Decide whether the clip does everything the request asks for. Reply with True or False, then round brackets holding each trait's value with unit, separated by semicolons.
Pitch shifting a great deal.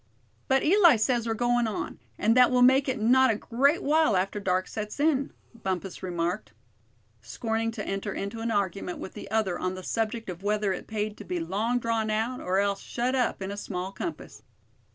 False (3.8 semitones)